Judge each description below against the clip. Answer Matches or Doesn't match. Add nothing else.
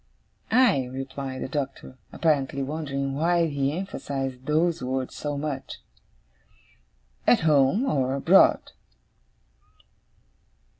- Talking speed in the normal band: Doesn't match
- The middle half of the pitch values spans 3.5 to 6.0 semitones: Doesn't match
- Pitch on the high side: Doesn't match